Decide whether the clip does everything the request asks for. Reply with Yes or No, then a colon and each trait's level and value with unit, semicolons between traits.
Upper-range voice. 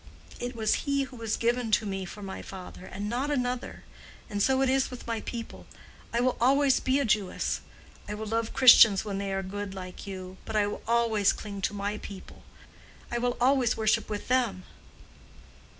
Yes: high, 220 Hz